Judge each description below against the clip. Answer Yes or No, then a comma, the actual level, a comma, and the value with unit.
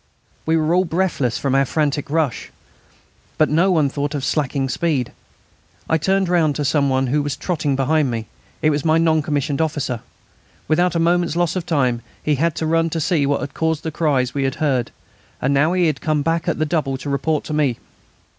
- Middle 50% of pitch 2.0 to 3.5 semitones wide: Yes, average, 2.9 semitones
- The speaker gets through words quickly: Yes, fast, 210 wpm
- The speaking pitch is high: No, medium, 150 Hz